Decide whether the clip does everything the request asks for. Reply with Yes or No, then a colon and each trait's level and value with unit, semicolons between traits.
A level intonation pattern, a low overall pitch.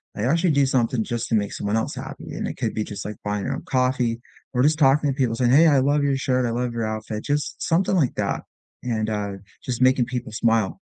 No: average, 3.6 semitones; low, 125 Hz